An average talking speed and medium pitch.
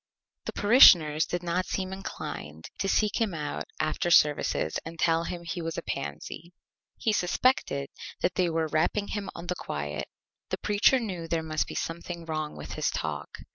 Yes: average, 175 wpm; medium, 170 Hz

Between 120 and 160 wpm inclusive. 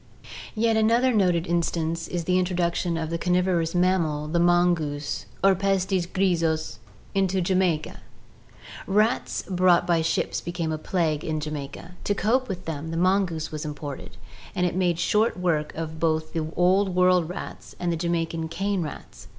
Yes: average, 155 wpm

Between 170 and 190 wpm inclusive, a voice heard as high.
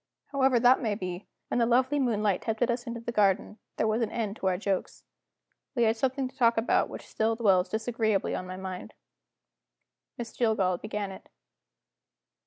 Yes: average, 180 wpm; high, 220 Hz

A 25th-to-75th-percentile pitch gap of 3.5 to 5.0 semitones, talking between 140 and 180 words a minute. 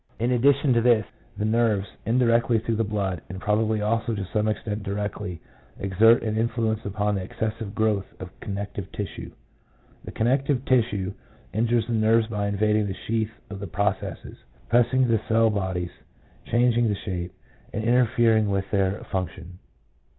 No: narrow, 2.5 semitones; average, 165 wpm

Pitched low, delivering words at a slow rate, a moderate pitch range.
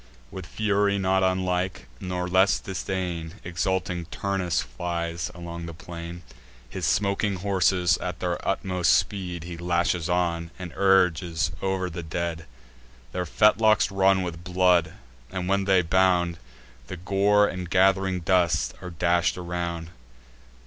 No: very low, 90 Hz; slow, 130 wpm; narrow, 1.8 semitones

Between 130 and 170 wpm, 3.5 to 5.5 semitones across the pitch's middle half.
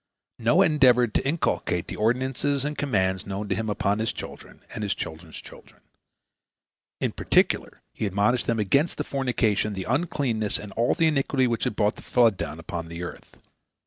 No: average, 180 wpm; average, 5.0 semitones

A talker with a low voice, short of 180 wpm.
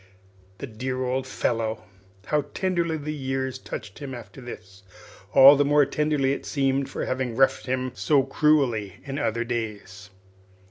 Yes: low, 130 Hz; average, 150 wpm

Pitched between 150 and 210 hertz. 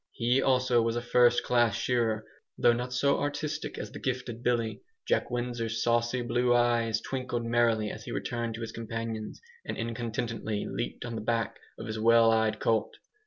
No: low, 115 Hz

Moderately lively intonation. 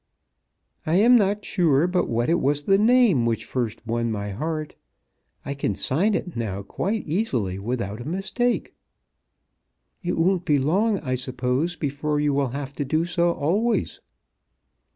No: wide, 6.6 semitones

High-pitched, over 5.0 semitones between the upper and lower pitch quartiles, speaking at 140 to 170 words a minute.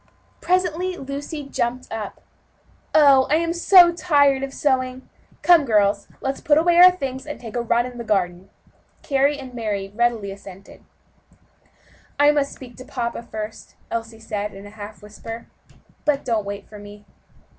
Yes: very high, 250 Hz; wide, 5.4 semitones; average, 155 wpm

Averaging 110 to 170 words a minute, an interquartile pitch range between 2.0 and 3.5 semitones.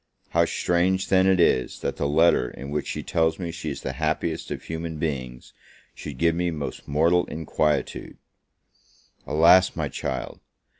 Yes: average, 160 wpm; average, 2.9 semitones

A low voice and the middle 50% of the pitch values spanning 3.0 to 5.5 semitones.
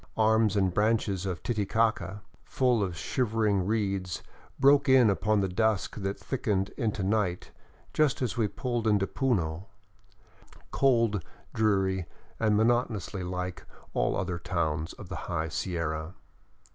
Yes: low, 100 Hz; average, 3.5 semitones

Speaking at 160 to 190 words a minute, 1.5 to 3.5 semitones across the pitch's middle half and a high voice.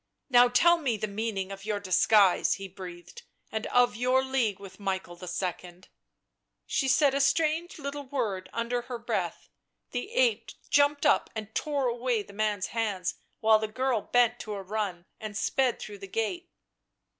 No: average, 175 wpm; average, 4.9 semitones; high, 225 Hz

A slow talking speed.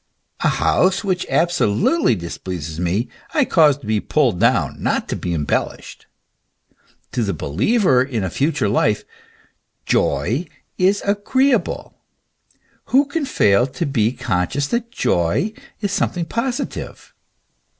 Yes: slow, 130 wpm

